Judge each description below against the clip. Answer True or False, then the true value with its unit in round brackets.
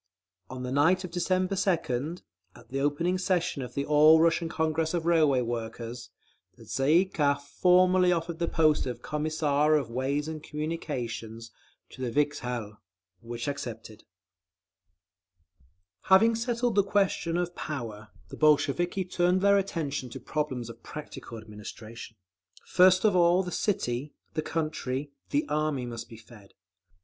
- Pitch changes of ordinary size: False (6.0 semitones)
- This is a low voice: False (150 Hz)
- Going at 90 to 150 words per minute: True (145 wpm)